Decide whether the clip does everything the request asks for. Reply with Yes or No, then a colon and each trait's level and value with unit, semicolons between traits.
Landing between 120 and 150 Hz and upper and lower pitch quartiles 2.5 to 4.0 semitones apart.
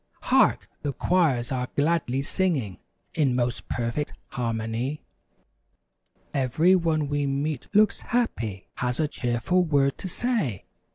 No: medium, 140 Hz; average, 5.3 semitones